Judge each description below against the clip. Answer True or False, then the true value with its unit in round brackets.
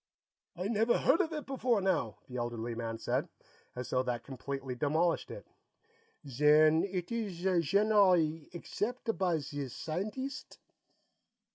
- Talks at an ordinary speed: False (130 wpm)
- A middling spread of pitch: False (7.5 semitones)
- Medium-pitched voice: True (170 Hz)